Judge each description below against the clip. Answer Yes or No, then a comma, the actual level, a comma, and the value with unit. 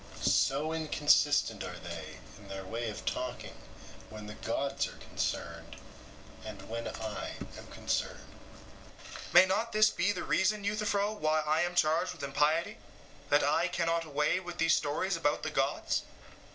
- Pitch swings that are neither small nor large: No, wide, 7.8 semitones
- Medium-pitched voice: Yes, medium, 155 Hz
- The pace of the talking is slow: No, average, 155 wpm